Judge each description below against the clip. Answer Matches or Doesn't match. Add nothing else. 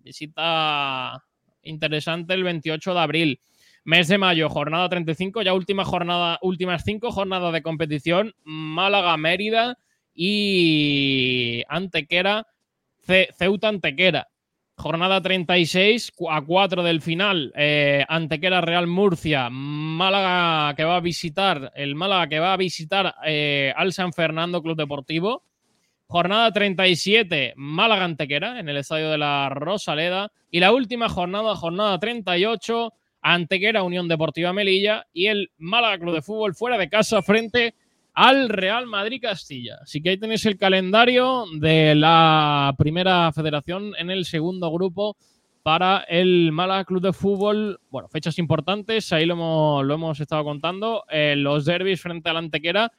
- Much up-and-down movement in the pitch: Doesn't match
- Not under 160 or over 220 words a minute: Doesn't match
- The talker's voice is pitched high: Doesn't match